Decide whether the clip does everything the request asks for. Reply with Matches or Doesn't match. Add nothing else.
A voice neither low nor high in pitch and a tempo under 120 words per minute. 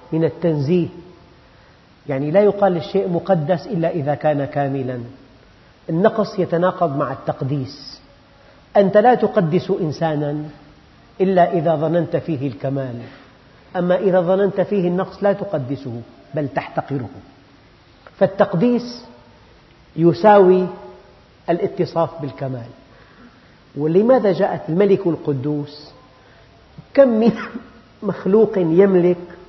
Matches